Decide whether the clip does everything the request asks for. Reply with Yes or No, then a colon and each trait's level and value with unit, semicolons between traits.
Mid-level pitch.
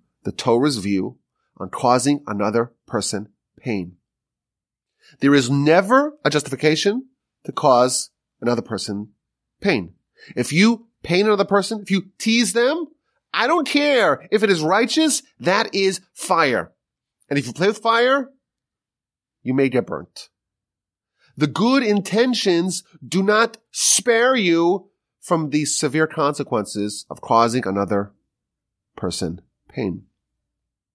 Yes: medium, 165 Hz